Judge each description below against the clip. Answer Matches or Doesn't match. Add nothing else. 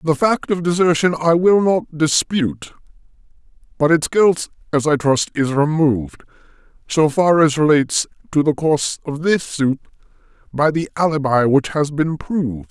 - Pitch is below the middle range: Doesn't match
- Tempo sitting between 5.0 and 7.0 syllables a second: Doesn't match